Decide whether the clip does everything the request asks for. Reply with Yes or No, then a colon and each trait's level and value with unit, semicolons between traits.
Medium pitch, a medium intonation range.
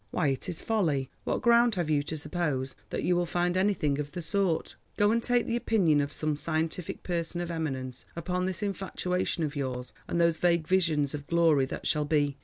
Yes: medium, 165 Hz; average, 3.7 semitones